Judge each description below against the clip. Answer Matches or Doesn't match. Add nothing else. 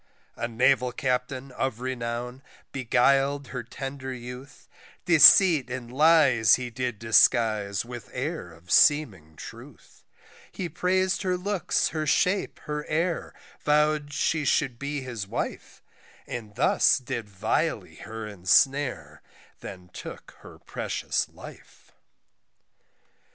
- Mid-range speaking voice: Doesn't match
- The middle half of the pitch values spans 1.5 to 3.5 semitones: Doesn't match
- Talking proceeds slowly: Matches